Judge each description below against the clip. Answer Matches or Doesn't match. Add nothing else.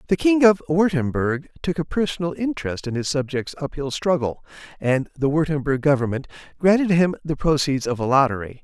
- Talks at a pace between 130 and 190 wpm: Matches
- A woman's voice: Doesn't match